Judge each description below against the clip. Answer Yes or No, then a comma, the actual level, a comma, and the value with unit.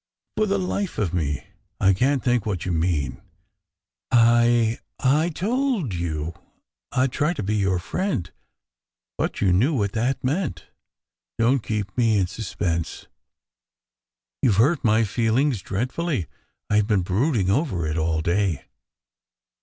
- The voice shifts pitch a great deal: Yes, wide, 6.7 semitones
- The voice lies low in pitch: Yes, low, 110 Hz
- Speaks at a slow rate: No, average, 155 wpm